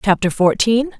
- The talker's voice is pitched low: No, high, 210 Hz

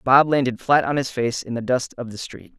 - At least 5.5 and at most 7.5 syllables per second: No, 5.3 syllables/s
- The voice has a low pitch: Yes, low, 125 Hz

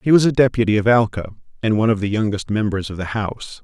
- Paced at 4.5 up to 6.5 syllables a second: No, 6.9 syllables/s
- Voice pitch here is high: No, low, 110 Hz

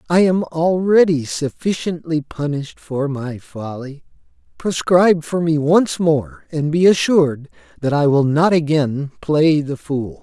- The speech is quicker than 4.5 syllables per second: No, 4.1 syllables/s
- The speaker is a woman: No, male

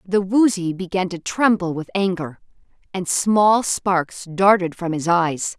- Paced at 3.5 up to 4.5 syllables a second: Yes, 3.9 syllables/s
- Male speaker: No, female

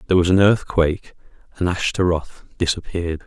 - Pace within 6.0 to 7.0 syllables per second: Yes, 6.1 syllables/s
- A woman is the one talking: No, male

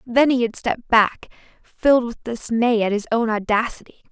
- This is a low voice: No, high, 230 Hz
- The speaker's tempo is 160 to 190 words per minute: Yes, average, 175 wpm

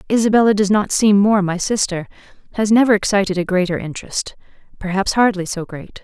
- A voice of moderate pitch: No, high, 200 Hz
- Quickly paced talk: No, average, 170 wpm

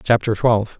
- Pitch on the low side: Yes, low, 110 Hz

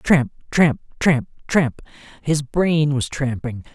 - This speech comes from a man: Yes, male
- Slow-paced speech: Yes, slow, 130 wpm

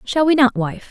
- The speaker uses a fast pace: Yes, fast, 265 wpm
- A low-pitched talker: No, very high, 250 Hz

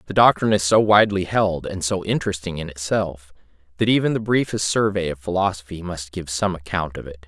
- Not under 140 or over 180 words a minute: No, average, 200 wpm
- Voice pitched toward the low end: Yes, very low, 90 Hz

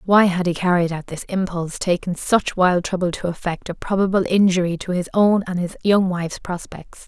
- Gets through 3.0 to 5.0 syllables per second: No, 5.3 syllables/s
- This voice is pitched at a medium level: Yes, medium, 180 Hz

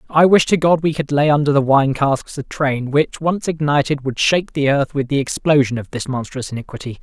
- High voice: No, medium, 140 Hz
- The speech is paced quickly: Yes, fast, 230 wpm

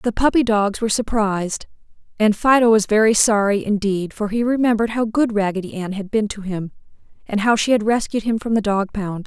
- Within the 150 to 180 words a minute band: No, fast, 205 wpm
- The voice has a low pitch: No, high, 215 Hz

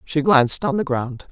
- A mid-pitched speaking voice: Yes, medium, 165 Hz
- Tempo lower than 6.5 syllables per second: Yes, 5.0 syllables/s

